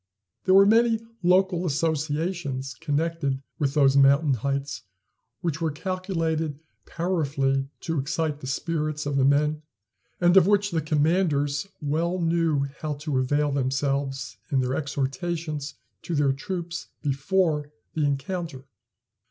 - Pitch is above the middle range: No, medium, 150 Hz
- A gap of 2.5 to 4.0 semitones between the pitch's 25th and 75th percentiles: Yes, average, 3.5 semitones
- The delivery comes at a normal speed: No, slow, 125 wpm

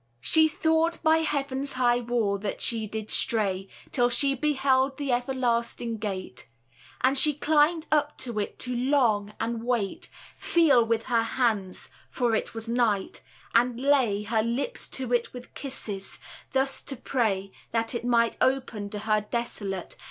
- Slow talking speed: No, average, 155 wpm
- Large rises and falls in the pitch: No, average, 3.6 semitones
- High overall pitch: Yes, high, 240 Hz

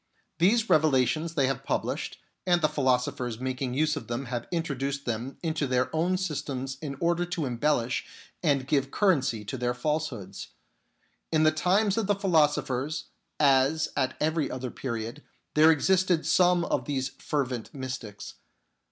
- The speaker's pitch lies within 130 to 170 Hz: Yes, medium, 140 Hz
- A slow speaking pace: No, average, 150 wpm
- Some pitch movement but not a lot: Yes, average, 3.9 semitones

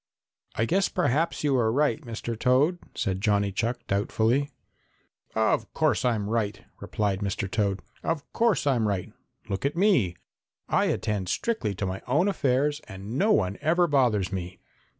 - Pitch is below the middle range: Yes, low, 115 Hz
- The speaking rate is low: No, average, 155 wpm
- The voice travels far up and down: Yes, wide, 6.5 semitones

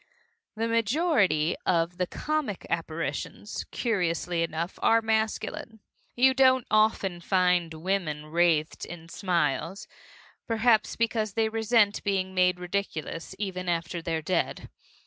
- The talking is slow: Yes, slow, 115 wpm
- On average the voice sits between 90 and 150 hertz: No, medium, 185 Hz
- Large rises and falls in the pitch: No, average, 4.7 semitones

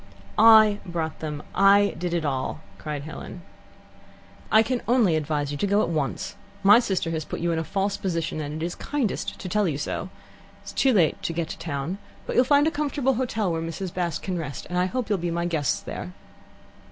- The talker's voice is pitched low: No, medium, 175 Hz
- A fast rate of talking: Yes, fast, 225 wpm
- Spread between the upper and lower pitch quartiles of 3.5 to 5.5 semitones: Yes, average, 4.6 semitones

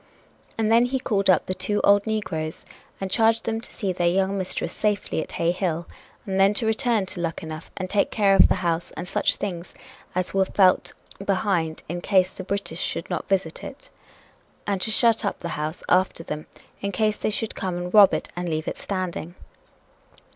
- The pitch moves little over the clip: No, average, 3.0 semitones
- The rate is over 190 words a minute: Yes, average, 200 wpm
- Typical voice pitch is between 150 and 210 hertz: Yes, high, 190 Hz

